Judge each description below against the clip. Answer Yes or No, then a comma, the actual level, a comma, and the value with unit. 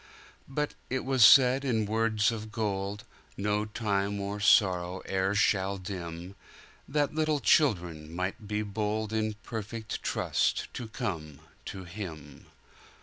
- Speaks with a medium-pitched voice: No, low, 105 Hz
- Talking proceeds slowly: Yes, slow, 115 wpm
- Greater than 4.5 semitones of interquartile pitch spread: No, average, 2.9 semitones